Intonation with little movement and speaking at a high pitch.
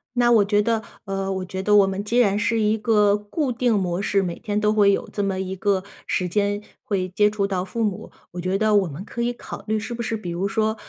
Yes: narrow, 2.2 semitones; high, 205 Hz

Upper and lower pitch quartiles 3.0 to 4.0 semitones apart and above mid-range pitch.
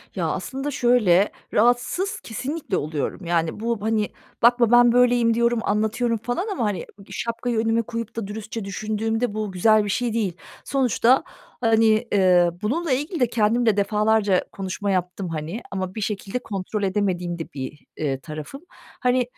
Yes: average, 3.7 semitones; high, 220 Hz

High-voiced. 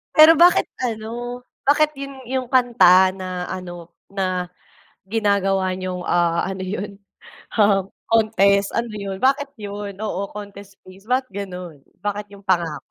Yes: high, 200 Hz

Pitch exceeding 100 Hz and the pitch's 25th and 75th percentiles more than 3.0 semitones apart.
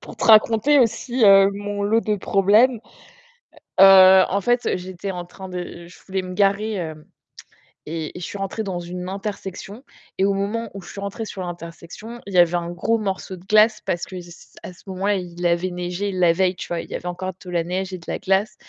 No: high, 190 Hz; narrow, 2.5 semitones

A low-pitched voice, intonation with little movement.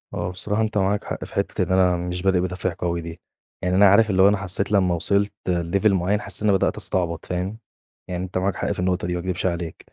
Yes: very low, 95 Hz; narrow, 1.9 semitones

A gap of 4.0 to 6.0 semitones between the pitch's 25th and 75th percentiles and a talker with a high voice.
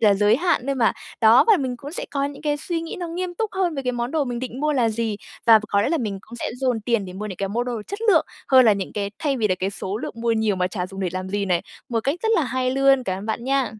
Yes: average, 5.1 semitones; high, 240 Hz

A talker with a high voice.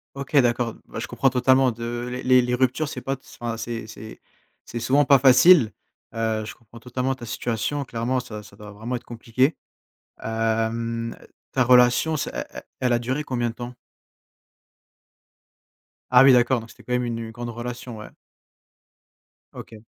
No: low, 120 Hz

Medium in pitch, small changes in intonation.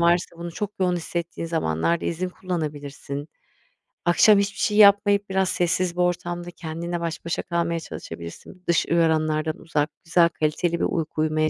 Yes: medium, 170 Hz; narrow, 2.2 semitones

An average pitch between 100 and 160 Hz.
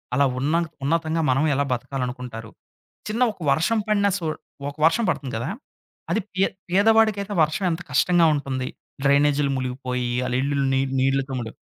Yes: medium, 140 Hz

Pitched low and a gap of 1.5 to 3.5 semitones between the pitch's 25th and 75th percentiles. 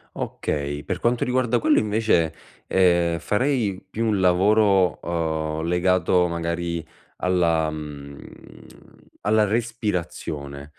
No: very low, 90 Hz; average, 4.7 semitones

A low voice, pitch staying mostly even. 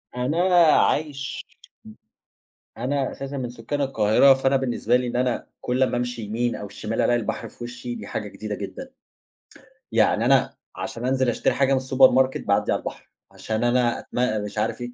Yes: low, 125 Hz; narrow, 2.3 semitones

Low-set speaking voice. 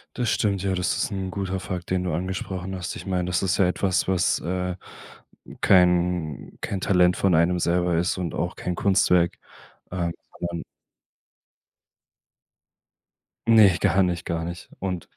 Yes: very low, 90 Hz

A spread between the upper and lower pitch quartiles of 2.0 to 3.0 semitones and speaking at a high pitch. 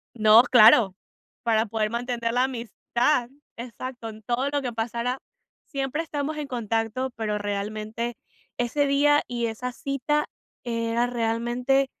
Yes: average, 2.7 semitones; high, 240 Hz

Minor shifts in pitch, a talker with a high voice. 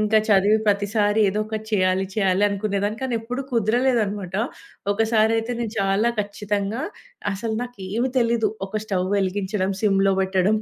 Yes: narrow, 2.3 semitones; high, 210 Hz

